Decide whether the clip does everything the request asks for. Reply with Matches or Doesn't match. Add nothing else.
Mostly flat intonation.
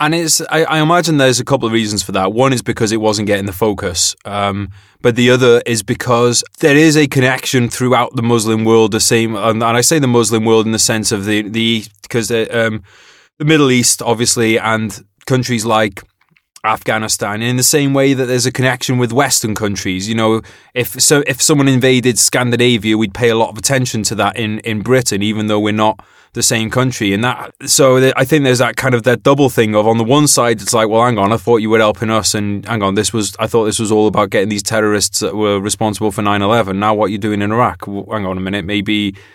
Doesn't match